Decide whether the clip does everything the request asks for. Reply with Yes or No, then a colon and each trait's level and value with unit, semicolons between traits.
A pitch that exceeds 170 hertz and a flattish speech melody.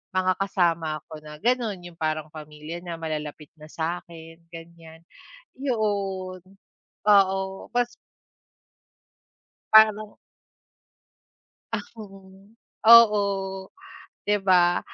No: medium, 185 Hz; average, 4.1 semitones